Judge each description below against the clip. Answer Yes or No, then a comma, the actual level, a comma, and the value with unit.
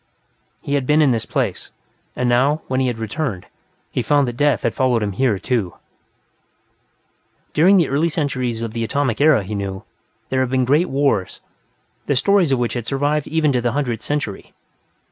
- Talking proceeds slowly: No, average, 185 wpm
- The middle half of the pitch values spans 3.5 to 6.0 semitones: Yes, average, 4.0 semitones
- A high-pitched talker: No, low, 130 Hz